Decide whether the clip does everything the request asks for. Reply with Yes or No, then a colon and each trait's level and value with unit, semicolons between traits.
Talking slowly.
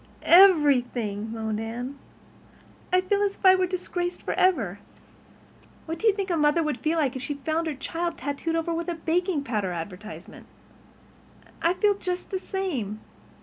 No: average, 165 wpm